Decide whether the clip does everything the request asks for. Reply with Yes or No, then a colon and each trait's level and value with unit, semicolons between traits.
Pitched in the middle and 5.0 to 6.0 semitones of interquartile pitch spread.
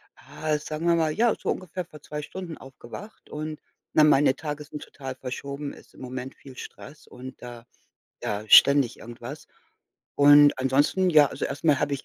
No: medium, 145 Hz; average, 2.7 semitones